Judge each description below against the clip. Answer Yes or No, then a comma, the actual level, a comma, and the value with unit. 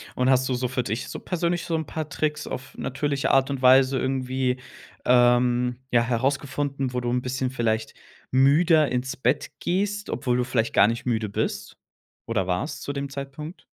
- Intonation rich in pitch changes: No, narrow, 2.5 semitones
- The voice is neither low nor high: No, low, 130 Hz